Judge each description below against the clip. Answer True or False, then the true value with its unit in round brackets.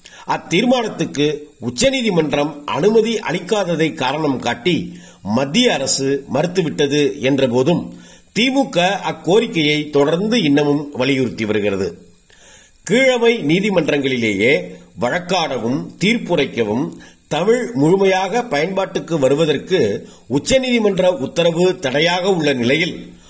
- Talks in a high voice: False (160 Hz)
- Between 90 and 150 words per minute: False (75 wpm)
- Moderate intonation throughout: False (6.3 semitones)